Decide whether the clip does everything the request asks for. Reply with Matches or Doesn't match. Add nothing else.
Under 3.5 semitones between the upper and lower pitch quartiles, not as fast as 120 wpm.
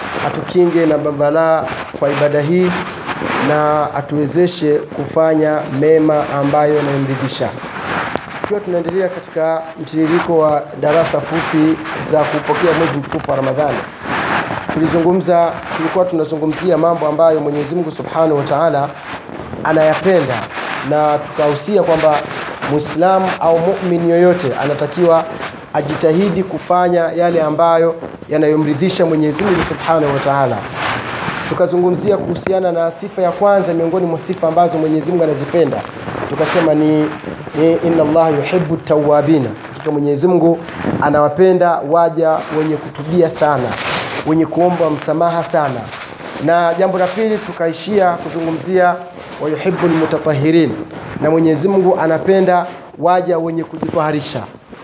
Matches